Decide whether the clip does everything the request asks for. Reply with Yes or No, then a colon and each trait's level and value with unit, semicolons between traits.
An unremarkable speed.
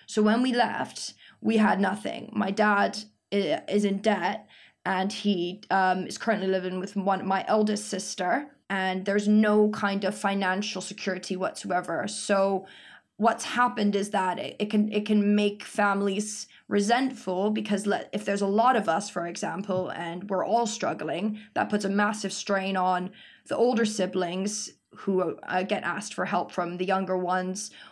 Yes: average, 165 wpm